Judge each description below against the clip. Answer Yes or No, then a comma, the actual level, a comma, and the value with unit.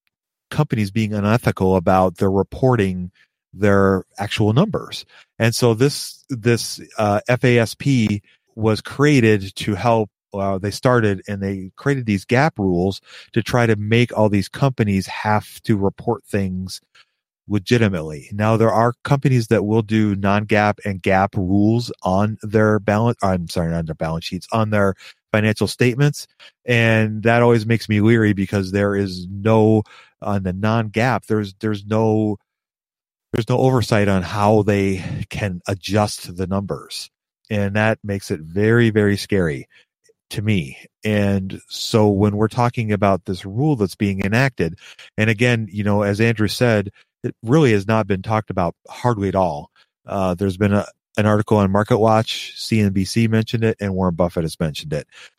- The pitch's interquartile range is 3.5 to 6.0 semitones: No, narrow, 2.6 semitones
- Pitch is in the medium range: No, low, 105 Hz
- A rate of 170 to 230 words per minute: No, average, 160 wpm